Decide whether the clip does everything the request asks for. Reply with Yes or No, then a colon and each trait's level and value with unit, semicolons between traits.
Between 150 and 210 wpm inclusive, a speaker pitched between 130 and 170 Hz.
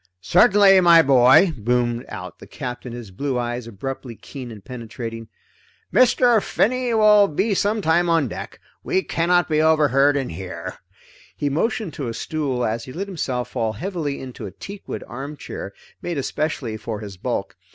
Yes: average, 160 wpm; medium, 140 Hz